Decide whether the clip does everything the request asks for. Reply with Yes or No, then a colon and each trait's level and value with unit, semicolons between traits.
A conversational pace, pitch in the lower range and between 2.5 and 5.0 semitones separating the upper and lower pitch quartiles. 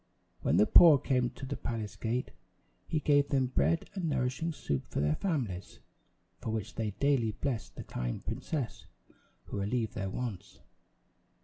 No: average, 155 wpm; low, 120 Hz; wide, 5.4 semitones